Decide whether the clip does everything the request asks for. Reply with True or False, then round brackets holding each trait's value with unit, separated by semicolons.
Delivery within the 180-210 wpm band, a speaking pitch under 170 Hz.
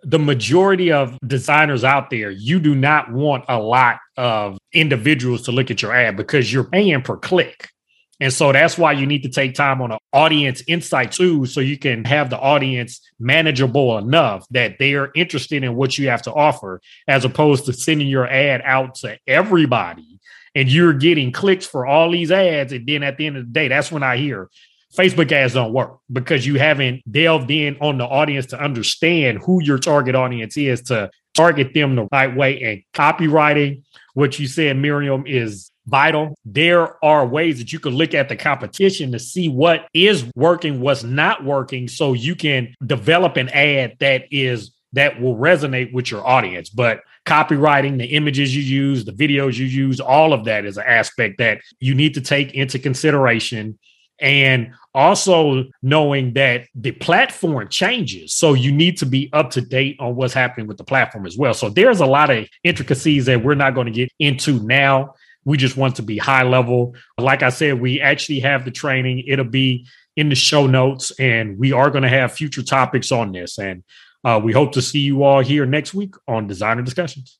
True (200 wpm; 135 Hz)